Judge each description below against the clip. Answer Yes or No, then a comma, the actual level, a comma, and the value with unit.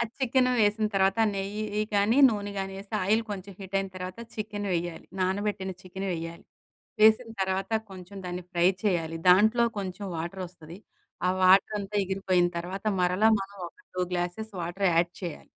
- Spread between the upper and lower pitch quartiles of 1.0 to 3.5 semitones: Yes, narrow, 2.4 semitones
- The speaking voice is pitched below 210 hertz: Yes, high, 195 Hz